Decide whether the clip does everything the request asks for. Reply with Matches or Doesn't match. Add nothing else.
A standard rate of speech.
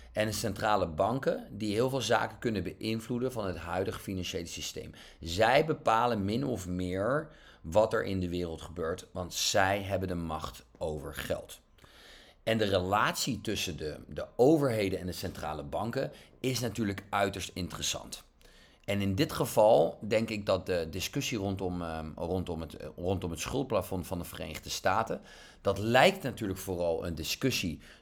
Matches